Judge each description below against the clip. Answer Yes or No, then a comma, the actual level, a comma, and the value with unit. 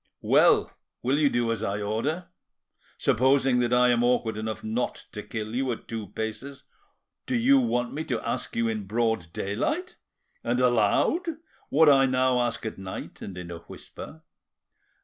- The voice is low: Yes, low, 120 Hz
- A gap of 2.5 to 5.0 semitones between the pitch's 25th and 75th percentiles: Yes, average, 3.6 semitones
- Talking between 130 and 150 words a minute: No, average, 170 wpm